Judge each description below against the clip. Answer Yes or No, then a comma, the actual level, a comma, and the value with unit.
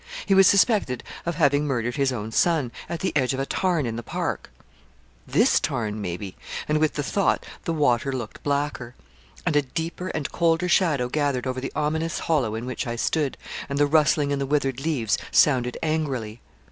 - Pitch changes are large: No, average, 4.2 semitones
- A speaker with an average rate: Yes, average, 190 wpm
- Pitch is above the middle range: No, medium, 140 Hz